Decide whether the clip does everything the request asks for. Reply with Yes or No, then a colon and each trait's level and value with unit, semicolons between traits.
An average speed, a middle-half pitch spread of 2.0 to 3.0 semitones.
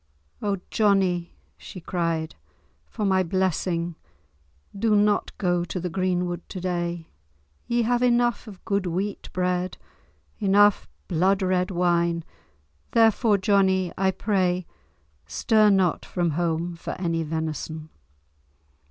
No: slow, 115 wpm; narrow, 2.6 semitones